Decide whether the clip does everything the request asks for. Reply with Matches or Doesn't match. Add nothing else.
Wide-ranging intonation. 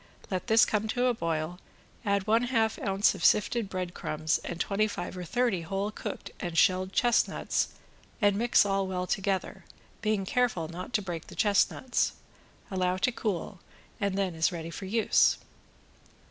Doesn't match